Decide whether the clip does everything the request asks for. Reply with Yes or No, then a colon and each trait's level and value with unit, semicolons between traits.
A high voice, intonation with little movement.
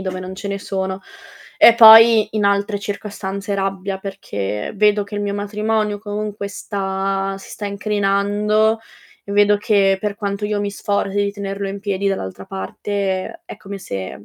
Yes: high, 200 Hz; narrow, 1.1 semitones